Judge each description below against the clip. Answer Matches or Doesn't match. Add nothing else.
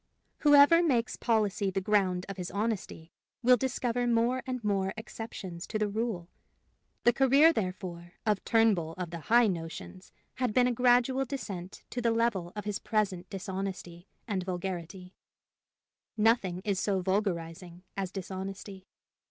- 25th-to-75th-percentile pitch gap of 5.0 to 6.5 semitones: Doesn't match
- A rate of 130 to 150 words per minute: Matches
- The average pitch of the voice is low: Doesn't match